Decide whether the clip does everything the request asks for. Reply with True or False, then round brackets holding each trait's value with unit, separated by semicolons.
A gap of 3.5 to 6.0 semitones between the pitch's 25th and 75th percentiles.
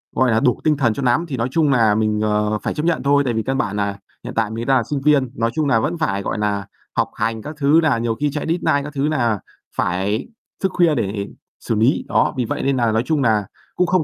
True (5.2 semitones)